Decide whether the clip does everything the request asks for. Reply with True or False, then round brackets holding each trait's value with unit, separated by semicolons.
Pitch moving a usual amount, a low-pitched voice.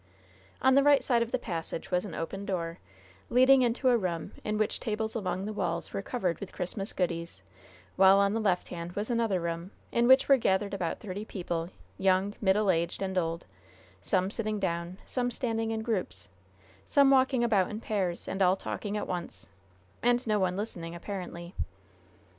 False (4.1 semitones; 200 Hz)